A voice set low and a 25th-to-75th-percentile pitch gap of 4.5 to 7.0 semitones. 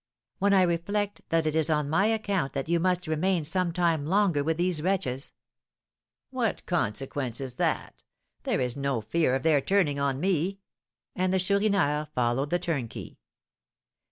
No: medium, 165 Hz; average, 4.8 semitones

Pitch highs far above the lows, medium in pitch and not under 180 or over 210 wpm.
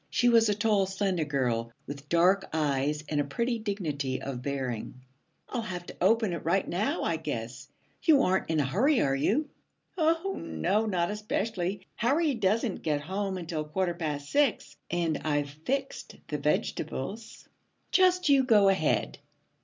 No: wide, 7.0 semitones; medium, 180 Hz; average, 160 wpm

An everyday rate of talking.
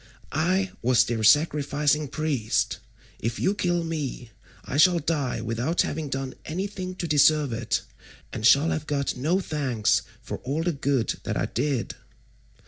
Yes: average, 150 wpm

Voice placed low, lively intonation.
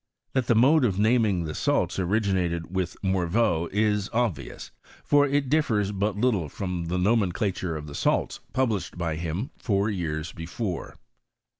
No: low, 100 Hz; average, 4.7 semitones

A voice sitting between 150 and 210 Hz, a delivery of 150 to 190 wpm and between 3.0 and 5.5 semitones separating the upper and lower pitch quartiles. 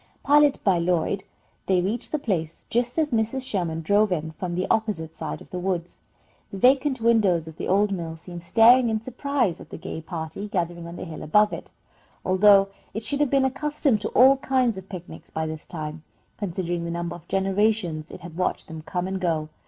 No: high, 190 Hz; fast, 205 wpm; average, 5.1 semitones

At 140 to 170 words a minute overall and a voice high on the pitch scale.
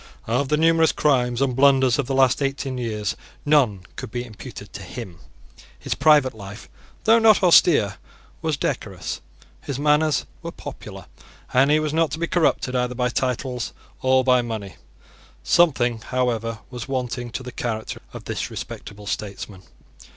No: average, 160 wpm; low, 130 Hz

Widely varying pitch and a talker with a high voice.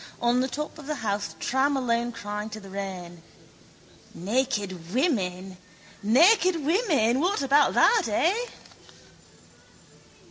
Yes: wide, 6.7 semitones; high, 240 Hz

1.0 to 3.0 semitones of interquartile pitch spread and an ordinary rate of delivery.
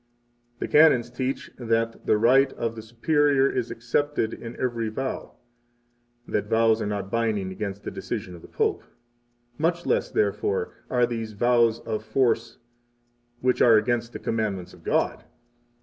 Yes: average, 2.7 semitones; average, 150 wpm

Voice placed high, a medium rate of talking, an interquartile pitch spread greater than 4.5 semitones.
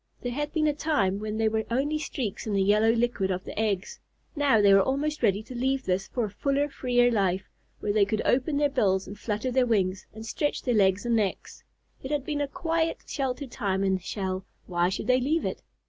No: high, 230 Hz; fast, 230 wpm; wide, 5.6 semitones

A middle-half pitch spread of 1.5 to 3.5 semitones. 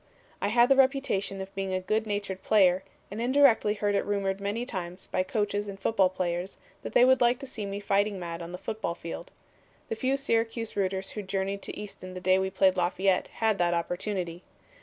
Yes: average, 2.9 semitones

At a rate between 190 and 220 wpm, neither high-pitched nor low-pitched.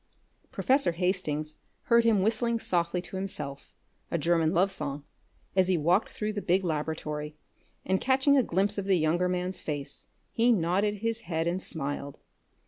No: average, 160 wpm; medium, 180 Hz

